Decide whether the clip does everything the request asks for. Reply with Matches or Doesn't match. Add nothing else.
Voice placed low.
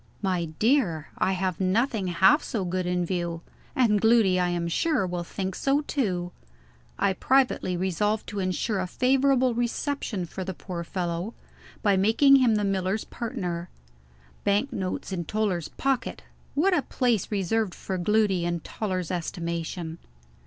Doesn't match